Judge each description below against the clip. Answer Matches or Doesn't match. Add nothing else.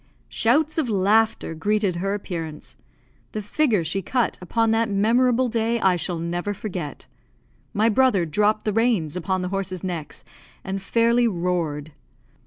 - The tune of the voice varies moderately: Matches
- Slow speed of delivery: Doesn't match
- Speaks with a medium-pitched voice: Doesn't match